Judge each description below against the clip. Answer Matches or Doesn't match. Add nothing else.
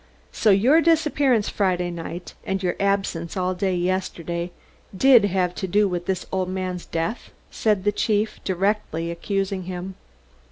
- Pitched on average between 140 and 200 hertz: Matches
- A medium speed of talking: Matches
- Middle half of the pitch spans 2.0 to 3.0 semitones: Matches